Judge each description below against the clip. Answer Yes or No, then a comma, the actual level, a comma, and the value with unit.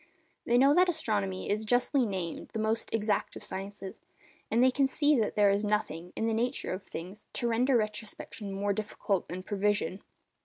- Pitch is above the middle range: Yes, high, 210 Hz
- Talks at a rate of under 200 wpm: Yes, average, 190 wpm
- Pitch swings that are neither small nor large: Yes, average, 3.4 semitones